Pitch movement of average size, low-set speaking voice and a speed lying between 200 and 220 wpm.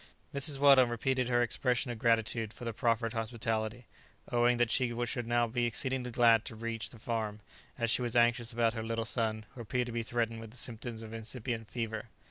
No: narrow, 1.4 semitones; low, 115 Hz; fast, 205 wpm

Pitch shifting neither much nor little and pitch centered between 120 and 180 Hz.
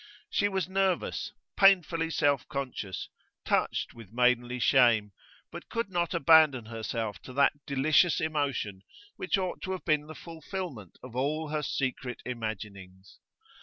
No: wide, 6.0 semitones; medium, 140 Hz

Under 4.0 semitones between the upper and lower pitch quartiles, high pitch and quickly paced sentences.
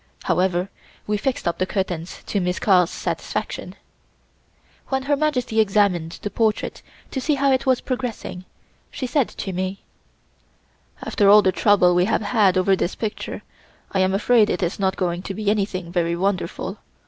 No: average, 3.3 semitones; high, 195 Hz; average, 170 wpm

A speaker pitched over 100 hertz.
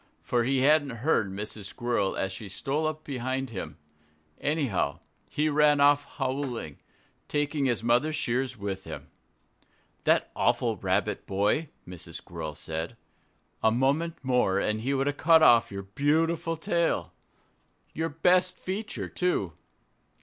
Yes: low, 135 Hz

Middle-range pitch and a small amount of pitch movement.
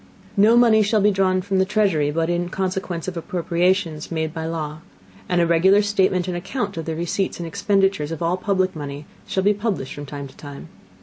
No: medium, 180 Hz; average, 3.3 semitones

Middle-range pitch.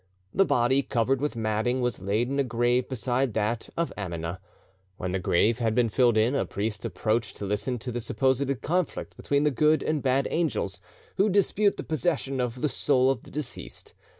No: low, 125 Hz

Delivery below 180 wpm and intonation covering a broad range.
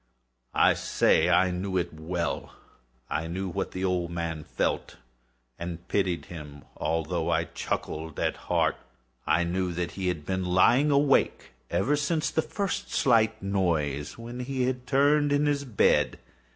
Yes: average, 150 wpm; wide, 6.9 semitones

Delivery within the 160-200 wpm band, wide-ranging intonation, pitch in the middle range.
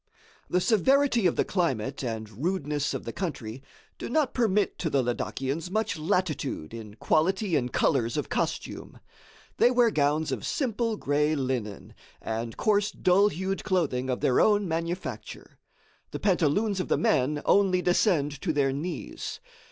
No: average, 150 wpm; wide, 6.8 semitones; medium, 165 Hz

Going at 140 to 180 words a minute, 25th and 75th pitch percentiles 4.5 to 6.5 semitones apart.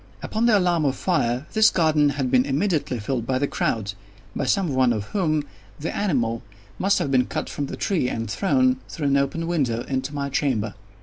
No: average, 195 wpm; average, 5.2 semitones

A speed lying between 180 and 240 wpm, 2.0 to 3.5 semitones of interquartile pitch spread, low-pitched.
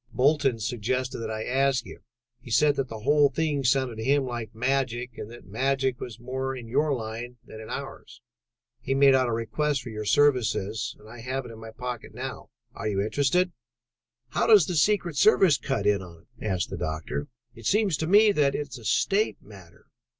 No: fast, 205 wpm; average, 3.9 semitones; low, 125 Hz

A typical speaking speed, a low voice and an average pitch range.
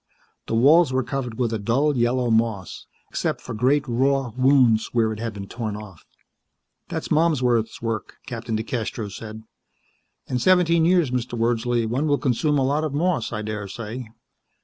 Yes: average, 165 wpm; low, 120 Hz; average, 3.5 semitones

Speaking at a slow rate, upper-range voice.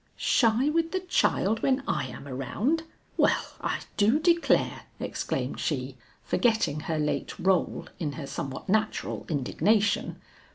Yes: slow, 130 wpm; high, 215 Hz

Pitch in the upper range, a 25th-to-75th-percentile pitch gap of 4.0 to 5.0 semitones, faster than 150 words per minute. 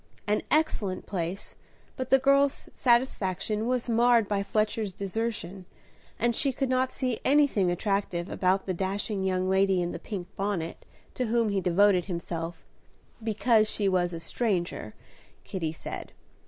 No: high, 200 Hz; average, 4.3 semitones; average, 145 wpm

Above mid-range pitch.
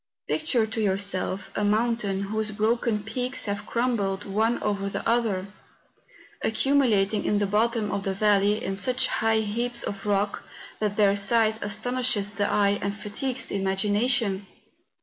Yes: high, 210 Hz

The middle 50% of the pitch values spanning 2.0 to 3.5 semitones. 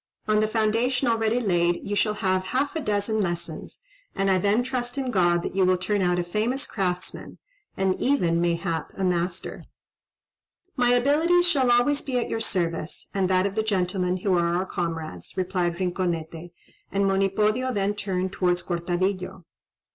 No: average, 4.1 semitones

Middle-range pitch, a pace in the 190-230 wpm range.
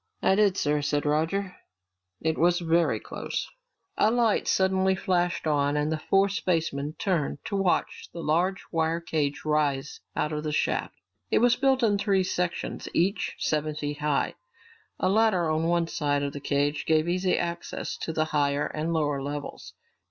No: medium, 160 Hz; average, 170 wpm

